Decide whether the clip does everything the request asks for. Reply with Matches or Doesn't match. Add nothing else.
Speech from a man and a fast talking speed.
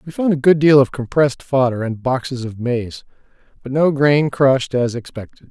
Doesn't match